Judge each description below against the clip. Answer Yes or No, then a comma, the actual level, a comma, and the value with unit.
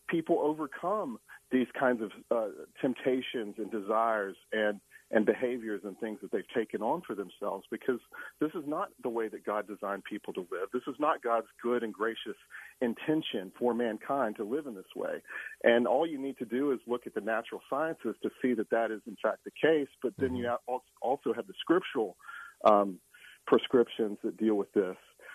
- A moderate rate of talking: Yes, average, 190 wpm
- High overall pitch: No, low, 120 Hz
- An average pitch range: Yes, average, 3.3 semitones